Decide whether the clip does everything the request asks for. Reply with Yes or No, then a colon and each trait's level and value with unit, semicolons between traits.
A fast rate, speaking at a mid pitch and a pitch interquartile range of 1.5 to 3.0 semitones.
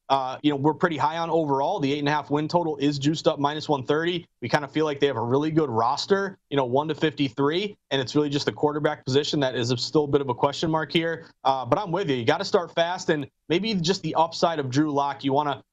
Yes: fast, 280 wpm; medium, 150 Hz; average, 2.7 semitones